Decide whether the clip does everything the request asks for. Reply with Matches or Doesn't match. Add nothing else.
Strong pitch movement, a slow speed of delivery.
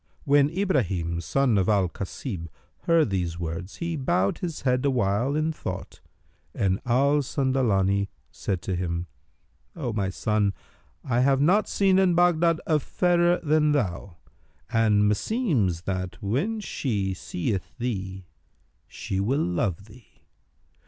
Matches